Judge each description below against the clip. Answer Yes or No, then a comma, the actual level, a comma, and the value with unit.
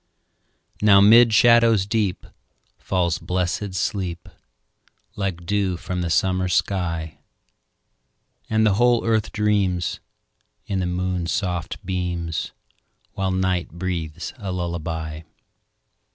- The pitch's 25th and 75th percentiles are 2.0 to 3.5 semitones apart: Yes, average, 2.8 semitones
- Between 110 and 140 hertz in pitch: No, very low, 95 Hz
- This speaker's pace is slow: Yes, slow, 105 wpm